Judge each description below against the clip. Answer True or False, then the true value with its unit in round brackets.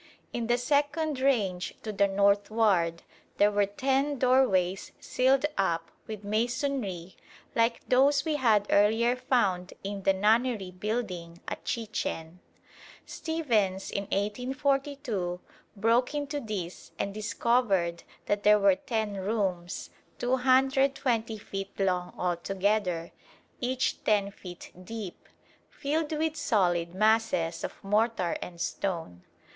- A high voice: True (210 Hz)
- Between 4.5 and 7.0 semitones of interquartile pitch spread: True (5.0 semitones)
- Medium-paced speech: False (115 wpm)